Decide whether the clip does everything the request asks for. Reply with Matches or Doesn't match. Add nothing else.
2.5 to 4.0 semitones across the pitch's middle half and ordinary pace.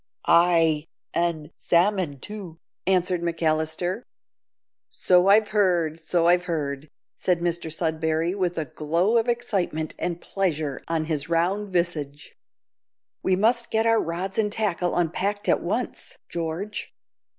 Doesn't match